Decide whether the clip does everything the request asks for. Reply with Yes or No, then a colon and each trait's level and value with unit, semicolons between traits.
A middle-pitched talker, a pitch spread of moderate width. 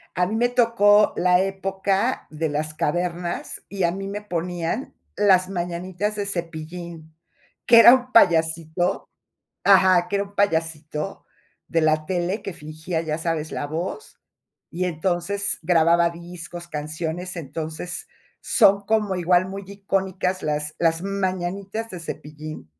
Yes: medium, 180 Hz; average, 3.3 semitones